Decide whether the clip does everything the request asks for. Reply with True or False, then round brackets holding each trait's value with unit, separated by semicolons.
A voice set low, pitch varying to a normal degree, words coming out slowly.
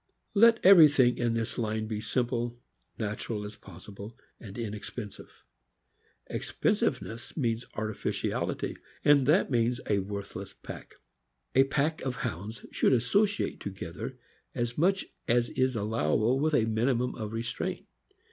True (115 Hz; 3.6 semitones; 130 wpm)